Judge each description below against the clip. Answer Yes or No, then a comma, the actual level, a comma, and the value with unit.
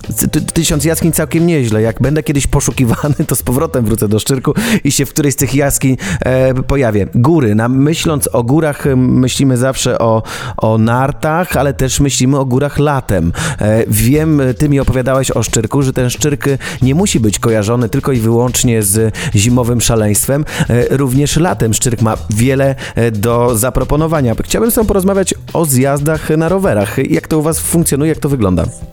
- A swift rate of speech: Yes, fast, 165 wpm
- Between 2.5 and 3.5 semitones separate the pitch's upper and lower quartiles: No, average, 4.4 semitones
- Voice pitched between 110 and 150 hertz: Yes, low, 135 Hz